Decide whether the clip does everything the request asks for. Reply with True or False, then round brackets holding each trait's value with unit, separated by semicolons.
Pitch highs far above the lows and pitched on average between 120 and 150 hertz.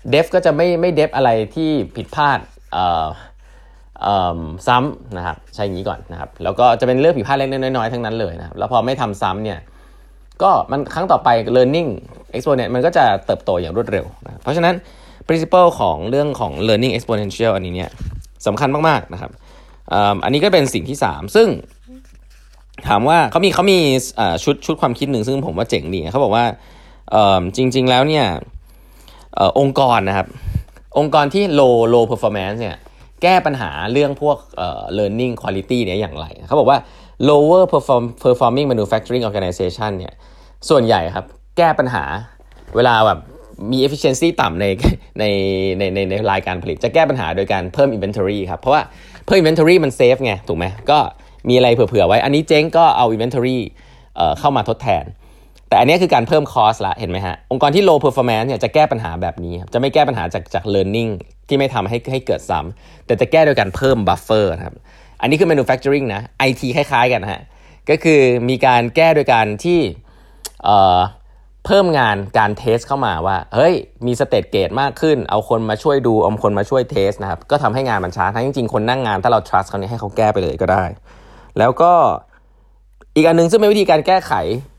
True (6.0 semitones; 125 Hz)